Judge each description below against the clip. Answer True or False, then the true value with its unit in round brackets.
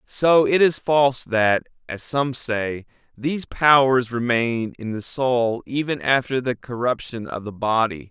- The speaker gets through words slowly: False (155 wpm)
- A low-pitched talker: True (125 Hz)